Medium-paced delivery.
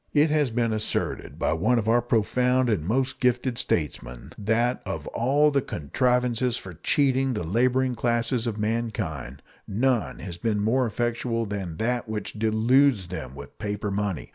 Yes: average, 160 wpm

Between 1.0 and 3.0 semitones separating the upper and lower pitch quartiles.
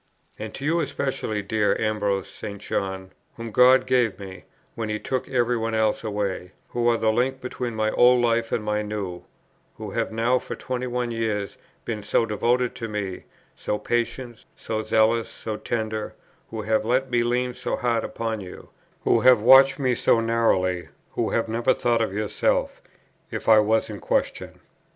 Yes: narrow, 2.5 semitones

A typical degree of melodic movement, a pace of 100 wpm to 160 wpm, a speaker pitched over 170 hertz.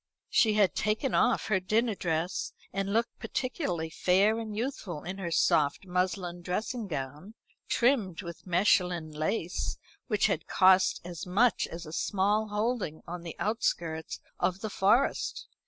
Yes: average, 4.0 semitones; average, 145 wpm; high, 190 Hz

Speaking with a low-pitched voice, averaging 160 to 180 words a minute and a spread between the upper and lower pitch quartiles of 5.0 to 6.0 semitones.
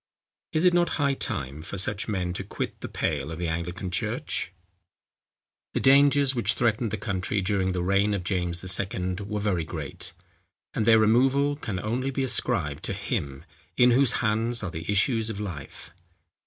Yes: low, 100 Hz; average, 175 wpm; average, 5.3 semitones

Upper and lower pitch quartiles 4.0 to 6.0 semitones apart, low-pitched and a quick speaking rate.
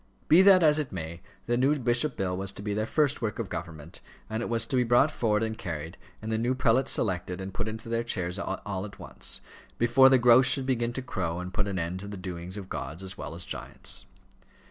Yes: average, 4.8 semitones; low, 110 Hz; fast, 240 wpm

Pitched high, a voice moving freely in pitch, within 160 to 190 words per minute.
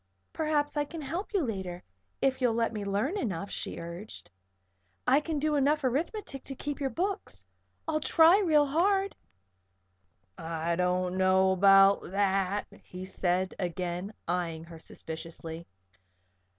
No: high, 205 Hz; wide, 8.5 semitones; slow, 135 wpm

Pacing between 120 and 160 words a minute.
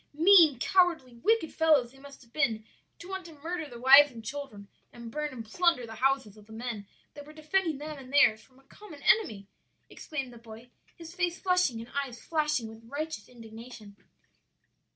No: average, 190 wpm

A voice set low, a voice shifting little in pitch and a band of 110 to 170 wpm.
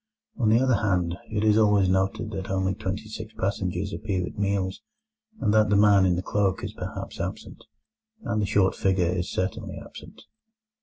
No: low, 100 Hz; narrow, 2.2 semitones; average, 185 wpm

